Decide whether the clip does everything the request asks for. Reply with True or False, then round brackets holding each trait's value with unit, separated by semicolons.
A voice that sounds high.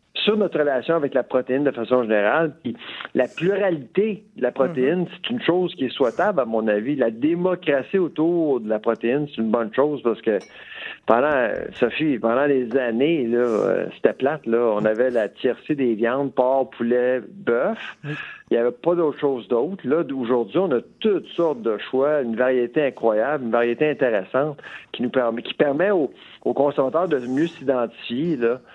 False (135 Hz)